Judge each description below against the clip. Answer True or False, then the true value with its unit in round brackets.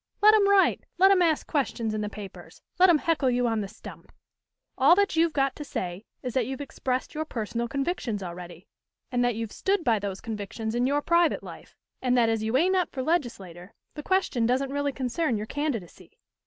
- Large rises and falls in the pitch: True (6.1 semitones)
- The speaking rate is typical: False (210 wpm)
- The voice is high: True (255 Hz)